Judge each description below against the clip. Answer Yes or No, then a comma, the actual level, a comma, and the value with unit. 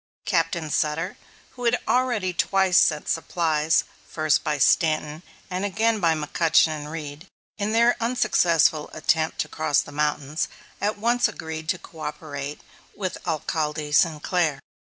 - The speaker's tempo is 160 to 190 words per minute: No, slow, 135 wpm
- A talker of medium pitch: Yes, medium, 160 Hz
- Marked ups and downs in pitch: No, average, 3.7 semitones